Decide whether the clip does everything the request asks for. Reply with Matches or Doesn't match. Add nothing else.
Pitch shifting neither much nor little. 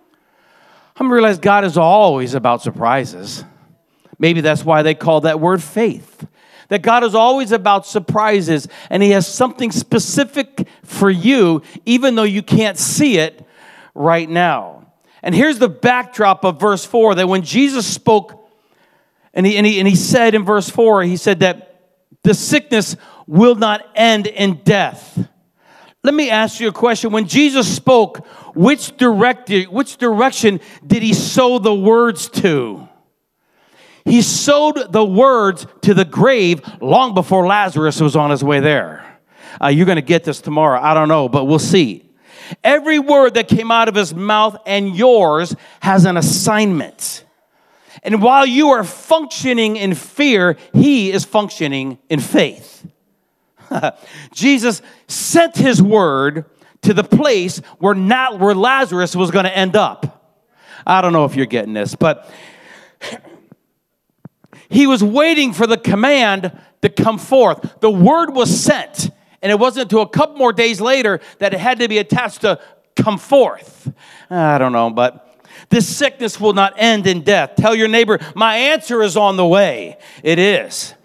Matches